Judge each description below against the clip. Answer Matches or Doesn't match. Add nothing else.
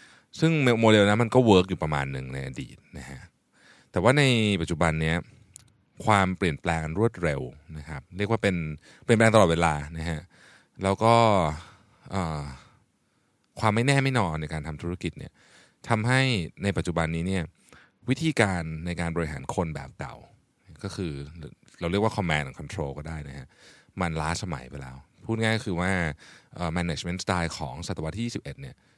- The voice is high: Doesn't match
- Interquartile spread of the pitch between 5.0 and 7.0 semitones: Matches